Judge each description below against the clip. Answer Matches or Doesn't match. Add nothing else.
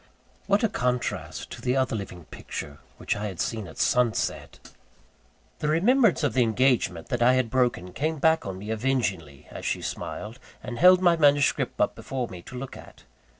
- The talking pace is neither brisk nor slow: Matches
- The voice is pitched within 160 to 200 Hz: Doesn't match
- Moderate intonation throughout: Doesn't match